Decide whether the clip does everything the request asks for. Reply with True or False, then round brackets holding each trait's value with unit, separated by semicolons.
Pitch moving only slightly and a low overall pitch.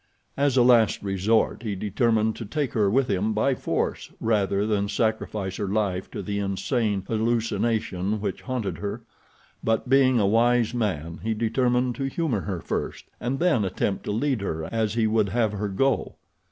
False (3.2 semitones; 110 Hz)